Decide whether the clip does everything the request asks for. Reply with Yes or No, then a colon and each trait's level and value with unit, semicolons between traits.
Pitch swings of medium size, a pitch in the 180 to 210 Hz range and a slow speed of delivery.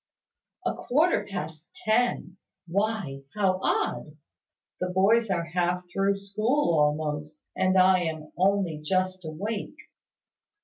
Yes: average, 3.8 semitones; medium, 185 Hz; slow, 115 wpm